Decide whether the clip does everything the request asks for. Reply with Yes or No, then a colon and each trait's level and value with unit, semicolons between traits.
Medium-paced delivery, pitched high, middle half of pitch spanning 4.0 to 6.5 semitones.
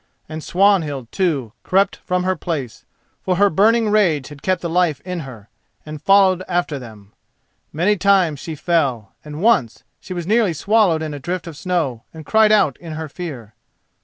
No: average, 180 wpm; medium, 170 Hz; average, 4.4 semitones